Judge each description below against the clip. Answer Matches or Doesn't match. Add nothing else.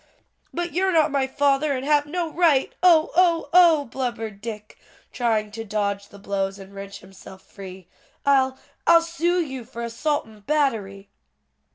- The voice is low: Doesn't match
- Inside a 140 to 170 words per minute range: Matches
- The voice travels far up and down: Matches